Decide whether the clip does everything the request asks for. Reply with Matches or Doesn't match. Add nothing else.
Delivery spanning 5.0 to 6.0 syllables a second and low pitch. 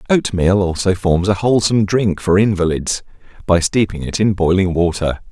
Matches